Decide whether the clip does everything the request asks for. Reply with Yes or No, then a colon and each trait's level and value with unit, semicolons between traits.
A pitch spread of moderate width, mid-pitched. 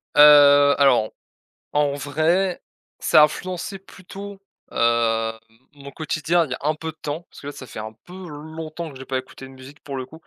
Yes: average, 3.2 semitones; medium, 145 Hz